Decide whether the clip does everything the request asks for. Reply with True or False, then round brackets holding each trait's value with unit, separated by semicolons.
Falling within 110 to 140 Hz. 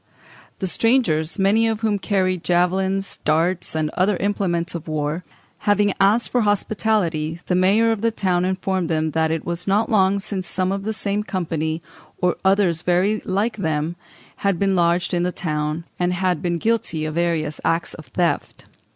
False (180 Hz)